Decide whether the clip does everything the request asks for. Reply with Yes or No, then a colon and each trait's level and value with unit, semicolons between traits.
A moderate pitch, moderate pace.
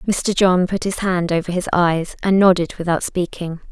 Yes: medium, 180 Hz; average, 195 wpm